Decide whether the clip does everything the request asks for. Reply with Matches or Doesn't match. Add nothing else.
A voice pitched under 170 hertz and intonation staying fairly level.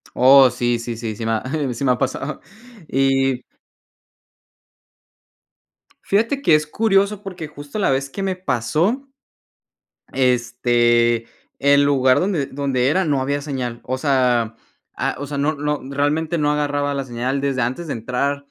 Doesn't match